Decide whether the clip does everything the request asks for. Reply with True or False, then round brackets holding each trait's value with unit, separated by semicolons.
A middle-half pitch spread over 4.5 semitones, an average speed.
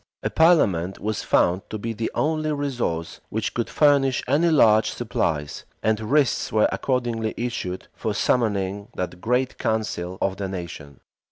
True (5.4 semitones; 150 wpm)